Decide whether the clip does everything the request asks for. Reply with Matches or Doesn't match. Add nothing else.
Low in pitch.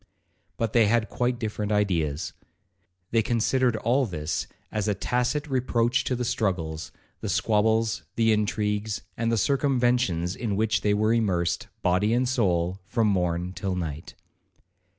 Matches